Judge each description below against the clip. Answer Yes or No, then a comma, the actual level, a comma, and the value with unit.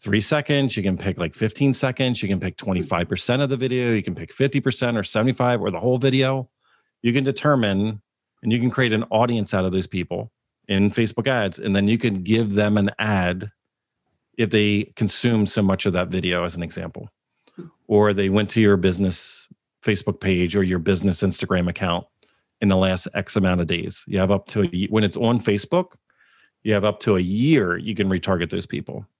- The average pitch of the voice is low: Yes, low, 105 Hz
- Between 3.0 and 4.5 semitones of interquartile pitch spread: Yes, average, 3.9 semitones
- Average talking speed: No, fast, 210 wpm